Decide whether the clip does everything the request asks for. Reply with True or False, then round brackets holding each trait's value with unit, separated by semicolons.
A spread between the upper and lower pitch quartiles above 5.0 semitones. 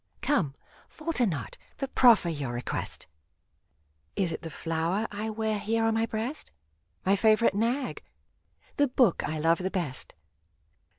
True (5.6 semitones)